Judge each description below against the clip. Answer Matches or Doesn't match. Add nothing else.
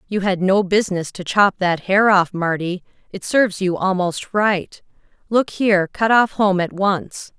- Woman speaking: Matches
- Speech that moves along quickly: Doesn't match